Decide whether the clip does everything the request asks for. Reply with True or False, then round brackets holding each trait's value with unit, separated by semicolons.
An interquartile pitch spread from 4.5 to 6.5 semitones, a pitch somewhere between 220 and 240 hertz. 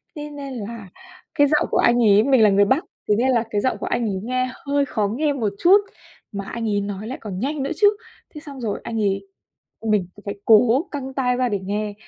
True (5.0 semitones; 235 Hz)